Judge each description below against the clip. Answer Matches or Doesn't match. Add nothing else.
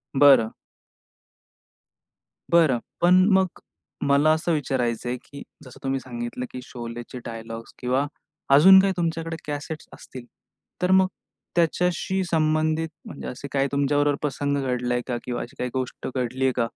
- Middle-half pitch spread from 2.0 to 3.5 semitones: Doesn't match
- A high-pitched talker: Doesn't match